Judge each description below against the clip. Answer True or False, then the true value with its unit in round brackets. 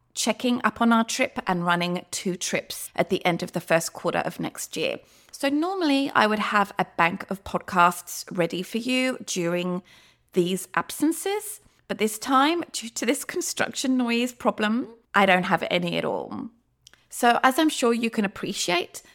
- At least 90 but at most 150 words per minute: False (175 wpm)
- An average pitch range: False (6.2 semitones)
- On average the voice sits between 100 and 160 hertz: False (215 Hz)